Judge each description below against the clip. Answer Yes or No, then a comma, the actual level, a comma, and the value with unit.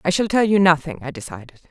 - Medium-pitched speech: Yes, medium, 165 Hz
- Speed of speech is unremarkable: No, fast, 245 wpm